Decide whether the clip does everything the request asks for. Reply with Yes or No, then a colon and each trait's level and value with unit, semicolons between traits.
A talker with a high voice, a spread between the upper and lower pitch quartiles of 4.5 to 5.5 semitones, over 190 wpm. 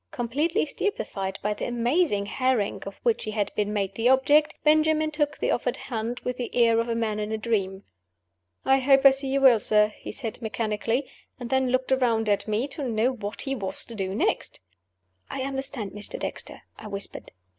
No: high, 235 Hz; average, 4.1 semitones; average, 200 wpm